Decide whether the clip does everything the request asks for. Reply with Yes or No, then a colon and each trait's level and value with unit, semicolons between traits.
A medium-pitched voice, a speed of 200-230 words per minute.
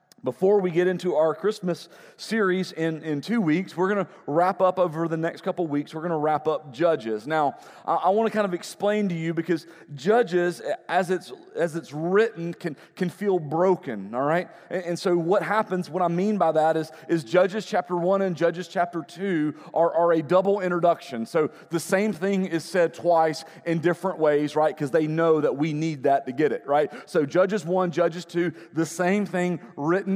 Yes: medium, 170 Hz; fast, 205 wpm